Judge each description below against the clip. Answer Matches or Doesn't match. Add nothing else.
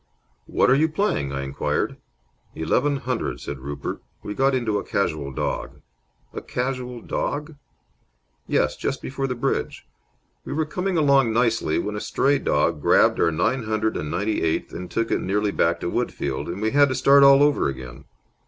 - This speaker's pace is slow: Doesn't match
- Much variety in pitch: Matches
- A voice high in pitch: Doesn't match